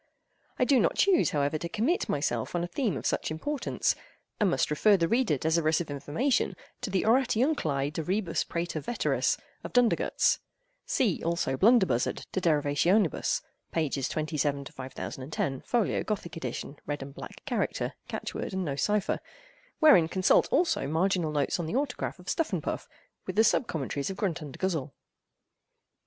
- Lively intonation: Yes, wide, 6.7 semitones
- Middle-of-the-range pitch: Yes, medium, 170 Hz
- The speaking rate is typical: Yes, average, 155 wpm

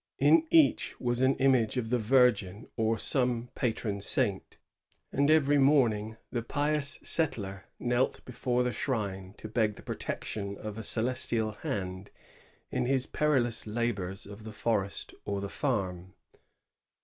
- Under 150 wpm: Yes, average, 140 wpm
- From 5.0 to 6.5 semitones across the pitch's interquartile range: No, average, 4.1 semitones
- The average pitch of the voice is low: Yes, low, 115 Hz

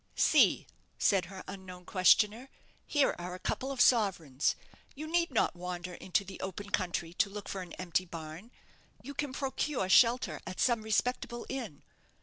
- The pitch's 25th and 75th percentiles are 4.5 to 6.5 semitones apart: Yes, wide, 5.6 semitones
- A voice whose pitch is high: Yes, high, 195 Hz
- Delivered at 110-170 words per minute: Yes, average, 160 wpm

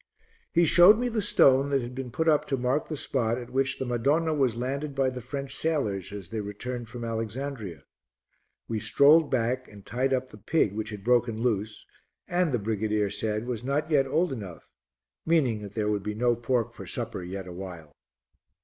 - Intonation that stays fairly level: No, average, 4.4 semitones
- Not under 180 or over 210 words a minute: Yes, average, 195 wpm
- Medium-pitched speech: No, low, 125 Hz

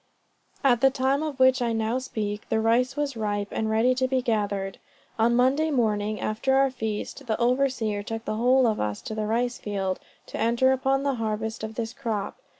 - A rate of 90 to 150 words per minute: No, average, 200 wpm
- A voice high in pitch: Yes, high, 230 Hz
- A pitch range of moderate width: Yes, average, 3.3 semitones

